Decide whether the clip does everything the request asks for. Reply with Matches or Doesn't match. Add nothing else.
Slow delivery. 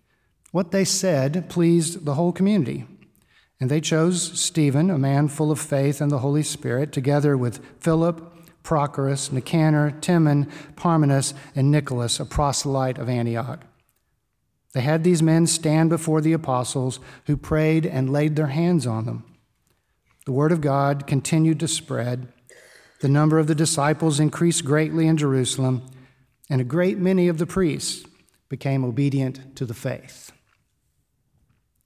Doesn't match